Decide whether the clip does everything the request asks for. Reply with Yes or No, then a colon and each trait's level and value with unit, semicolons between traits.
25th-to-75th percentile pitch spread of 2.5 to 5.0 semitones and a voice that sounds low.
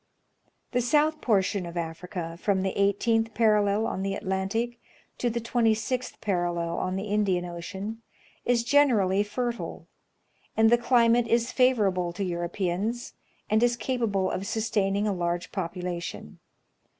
No: average, 4.1 semitones; high, 205 Hz